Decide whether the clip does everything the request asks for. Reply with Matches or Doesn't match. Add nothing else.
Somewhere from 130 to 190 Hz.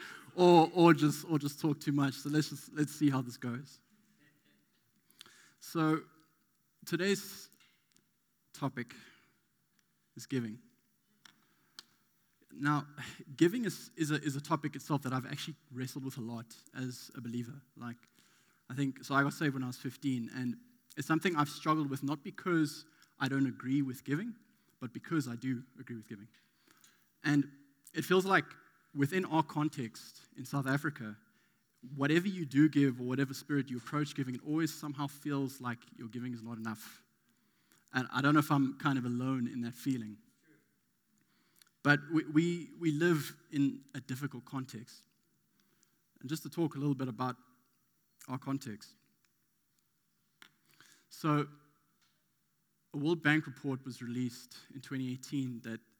Matches